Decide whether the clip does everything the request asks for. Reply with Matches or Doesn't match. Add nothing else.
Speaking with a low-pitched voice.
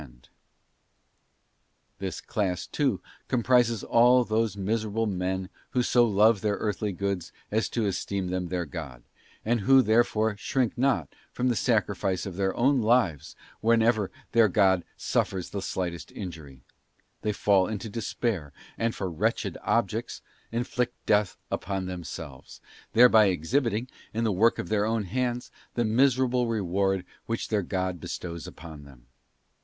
Matches